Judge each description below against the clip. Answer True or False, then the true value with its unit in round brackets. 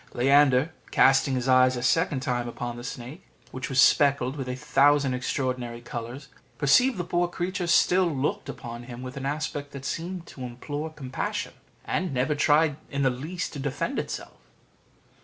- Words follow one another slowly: False (170 wpm)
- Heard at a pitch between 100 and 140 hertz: True (135 Hz)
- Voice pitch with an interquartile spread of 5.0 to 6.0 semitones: False (3.1 semitones)